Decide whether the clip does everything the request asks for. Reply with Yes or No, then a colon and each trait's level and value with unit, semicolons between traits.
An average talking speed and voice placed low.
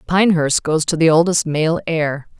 No: average, 175 wpm; medium, 160 Hz